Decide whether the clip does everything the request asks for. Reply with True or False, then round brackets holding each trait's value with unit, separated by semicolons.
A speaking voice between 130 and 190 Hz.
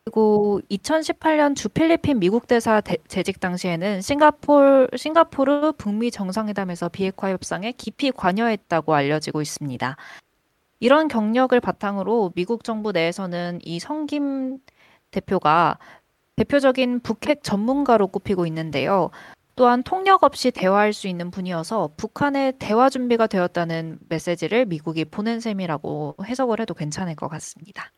False (215 Hz)